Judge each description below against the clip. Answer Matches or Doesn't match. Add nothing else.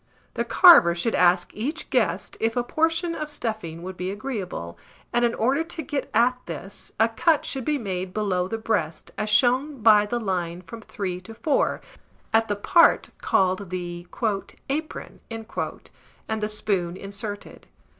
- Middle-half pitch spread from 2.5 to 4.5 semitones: Doesn't match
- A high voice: Matches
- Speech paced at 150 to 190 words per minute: Matches